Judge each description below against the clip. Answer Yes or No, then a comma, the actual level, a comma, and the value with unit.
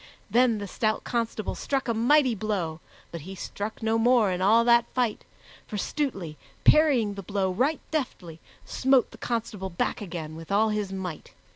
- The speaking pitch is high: Yes, high, 215 Hz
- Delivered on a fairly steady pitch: No, average, 4.1 semitones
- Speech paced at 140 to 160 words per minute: No, average, 170 wpm